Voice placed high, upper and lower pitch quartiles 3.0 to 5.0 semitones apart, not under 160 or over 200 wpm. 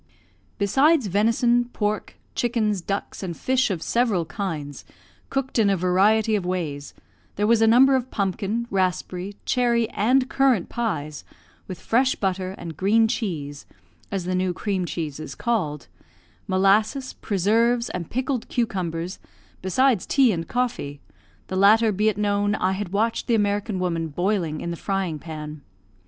No: high, 200 Hz; average, 4.3 semitones; average, 150 wpm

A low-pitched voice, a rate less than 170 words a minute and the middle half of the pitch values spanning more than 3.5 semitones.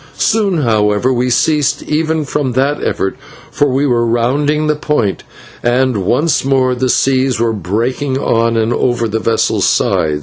Yes: low, 130 Hz; average, 160 wpm; average, 4.0 semitones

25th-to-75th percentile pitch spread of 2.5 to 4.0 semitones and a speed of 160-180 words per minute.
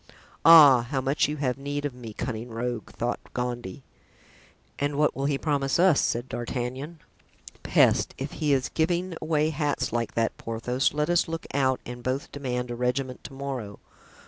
Yes: average, 3.2 semitones; average, 170 wpm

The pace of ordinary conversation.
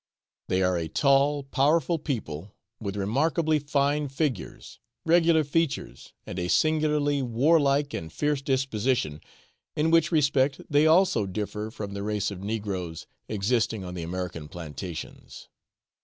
No: slow, 130 wpm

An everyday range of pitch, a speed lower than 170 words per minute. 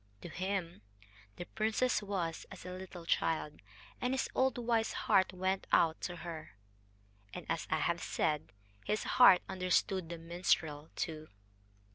Yes: average, 3.1 semitones; average, 145 wpm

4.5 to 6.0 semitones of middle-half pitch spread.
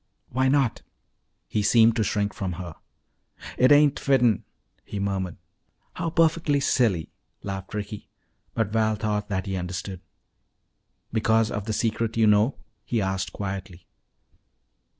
No: average, 3.3 semitones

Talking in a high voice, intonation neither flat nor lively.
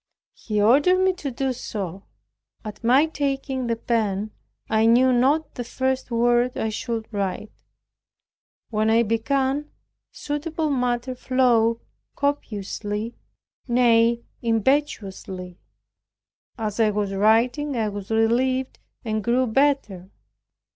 Yes: high, 235 Hz; average, 3.4 semitones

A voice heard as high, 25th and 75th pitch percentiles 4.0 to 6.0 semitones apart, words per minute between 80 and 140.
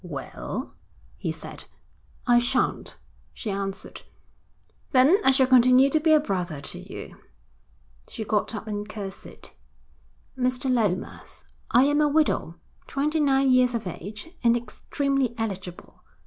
Yes: high, 245 Hz; average, 4.8 semitones; slow, 135 wpm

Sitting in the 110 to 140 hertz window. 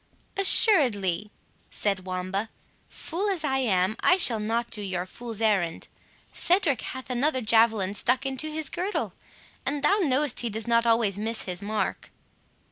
No: high, 230 Hz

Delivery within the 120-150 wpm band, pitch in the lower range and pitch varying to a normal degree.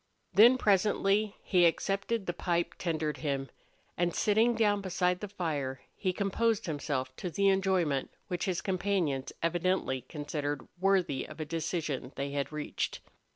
No: average, 145 wpm; medium, 175 Hz; average, 5.0 semitones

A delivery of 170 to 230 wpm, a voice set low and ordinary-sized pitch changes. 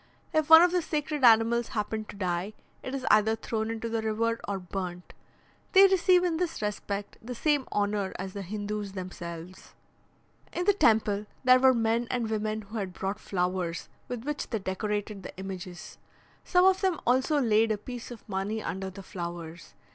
No: average, 180 wpm; high, 215 Hz; average, 4.6 semitones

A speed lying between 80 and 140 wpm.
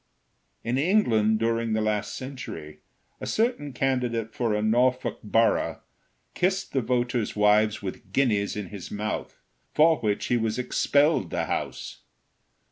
Yes: slow, 135 wpm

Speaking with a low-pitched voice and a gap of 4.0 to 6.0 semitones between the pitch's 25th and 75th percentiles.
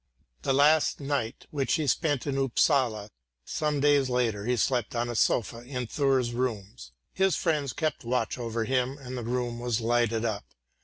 No: low, 125 Hz; average, 3.2 semitones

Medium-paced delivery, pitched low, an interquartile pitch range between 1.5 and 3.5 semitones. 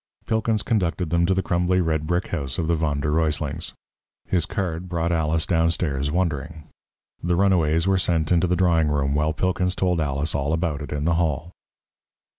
Yes: average, 185 wpm; very low, 85 Hz; narrow, 2.6 semitones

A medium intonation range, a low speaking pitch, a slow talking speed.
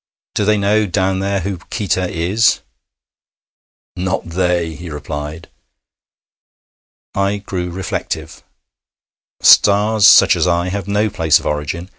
Yes: average, 3.2 semitones; very low, 95 Hz; slow, 120 wpm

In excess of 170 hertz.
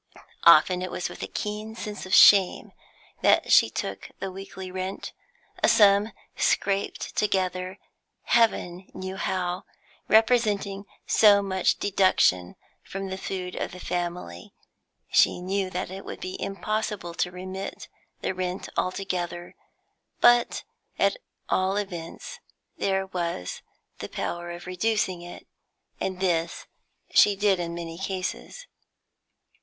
Yes: high, 190 Hz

